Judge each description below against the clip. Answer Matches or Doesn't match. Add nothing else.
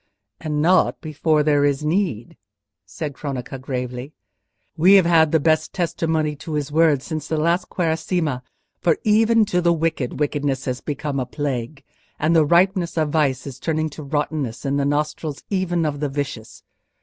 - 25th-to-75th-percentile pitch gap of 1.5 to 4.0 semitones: Matches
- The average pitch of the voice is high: Doesn't match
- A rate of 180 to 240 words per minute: Doesn't match